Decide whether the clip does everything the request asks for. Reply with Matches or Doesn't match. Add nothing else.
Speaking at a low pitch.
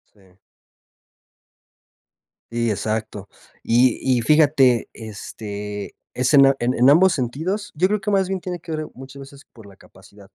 Matches